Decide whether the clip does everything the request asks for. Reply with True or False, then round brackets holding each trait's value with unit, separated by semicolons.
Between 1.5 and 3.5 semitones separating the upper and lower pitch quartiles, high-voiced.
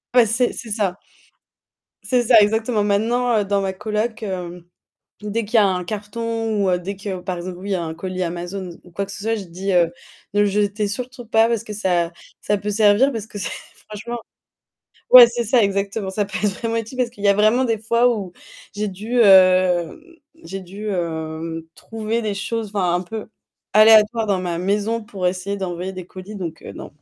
True (3.2 semitones; 205 Hz)